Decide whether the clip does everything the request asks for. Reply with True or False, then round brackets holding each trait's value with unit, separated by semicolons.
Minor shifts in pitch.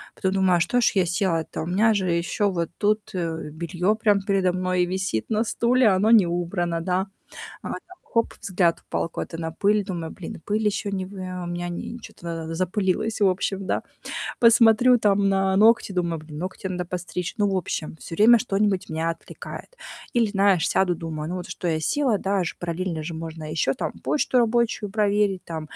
False (3.5 semitones)